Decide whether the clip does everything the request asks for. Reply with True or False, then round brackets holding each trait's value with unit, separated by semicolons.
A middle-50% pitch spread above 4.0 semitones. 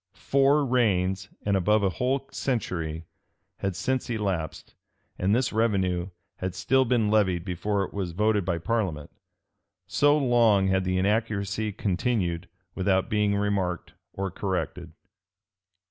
False (3.4 semitones)